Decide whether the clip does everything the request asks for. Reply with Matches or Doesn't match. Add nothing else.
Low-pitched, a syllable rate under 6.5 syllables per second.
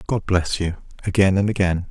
Matches